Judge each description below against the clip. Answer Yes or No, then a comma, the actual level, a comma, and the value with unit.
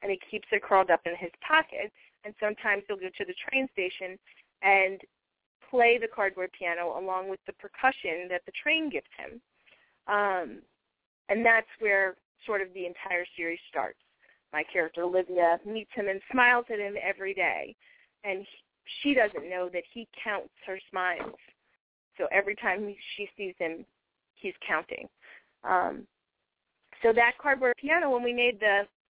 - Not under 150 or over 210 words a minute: Yes, average, 165 wpm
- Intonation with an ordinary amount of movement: Yes, average, 4.1 semitones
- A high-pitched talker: Yes, high, 200 Hz